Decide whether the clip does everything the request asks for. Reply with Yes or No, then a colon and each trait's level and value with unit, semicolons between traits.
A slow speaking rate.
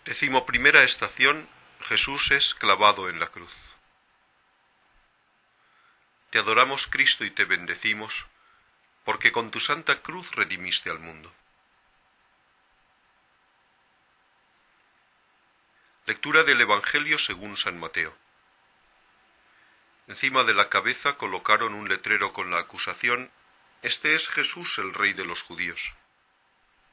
Yes: slow, 105 wpm